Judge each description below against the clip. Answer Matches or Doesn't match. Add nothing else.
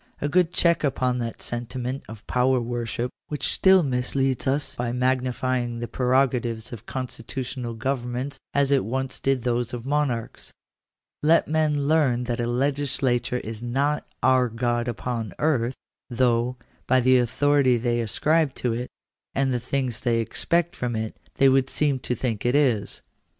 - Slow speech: Doesn't match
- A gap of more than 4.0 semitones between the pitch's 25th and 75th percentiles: Doesn't match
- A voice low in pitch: Matches